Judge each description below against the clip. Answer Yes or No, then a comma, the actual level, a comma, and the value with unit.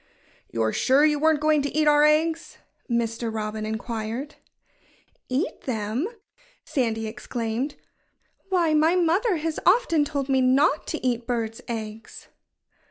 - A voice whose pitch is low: No, very high, 265 Hz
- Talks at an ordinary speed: No, slow, 130 wpm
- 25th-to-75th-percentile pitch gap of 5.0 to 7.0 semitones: Yes, average, 5.3 semitones